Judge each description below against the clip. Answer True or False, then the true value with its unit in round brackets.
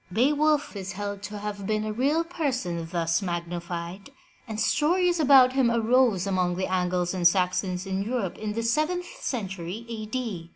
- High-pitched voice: True (205 Hz)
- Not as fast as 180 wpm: True (170 wpm)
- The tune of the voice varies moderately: False (5.9 semitones)